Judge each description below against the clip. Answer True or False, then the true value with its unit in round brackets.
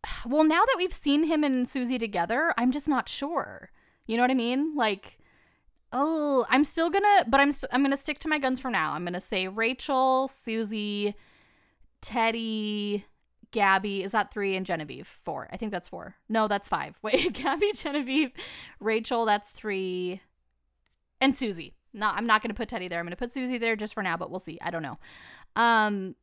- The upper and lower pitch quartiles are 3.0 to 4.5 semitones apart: False (5.2 semitones)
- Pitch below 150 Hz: False (230 Hz)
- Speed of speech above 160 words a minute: True (200 wpm)